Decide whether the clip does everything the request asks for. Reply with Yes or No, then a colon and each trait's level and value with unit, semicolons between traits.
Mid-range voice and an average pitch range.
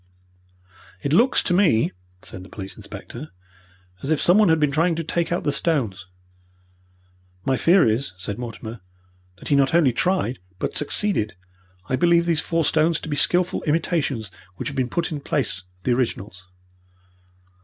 No: medium, 145 Hz; wide, 6.2 semitones